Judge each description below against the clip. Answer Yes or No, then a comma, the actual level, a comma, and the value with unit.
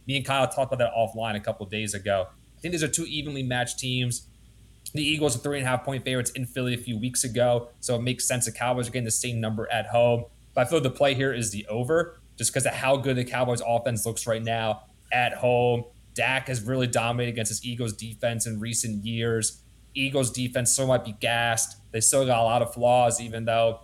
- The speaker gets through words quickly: Yes, fast, 240 wpm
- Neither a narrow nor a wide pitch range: No, narrow, 2.1 semitones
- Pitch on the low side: Yes, low, 120 Hz